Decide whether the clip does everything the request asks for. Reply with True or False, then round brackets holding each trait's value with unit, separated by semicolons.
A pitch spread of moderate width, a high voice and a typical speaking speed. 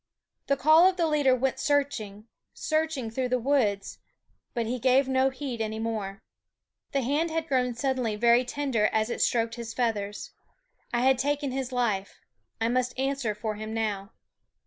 True (3.6 semitones; 250 Hz; 170 wpm)